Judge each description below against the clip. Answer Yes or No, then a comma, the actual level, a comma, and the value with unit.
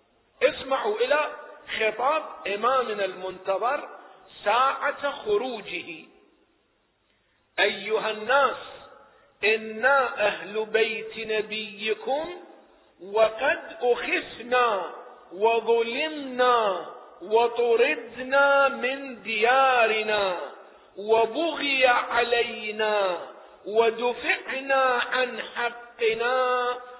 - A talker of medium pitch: No, high, 235 Hz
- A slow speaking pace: Yes, slow, 55 wpm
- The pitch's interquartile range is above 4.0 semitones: No, average, 3.0 semitones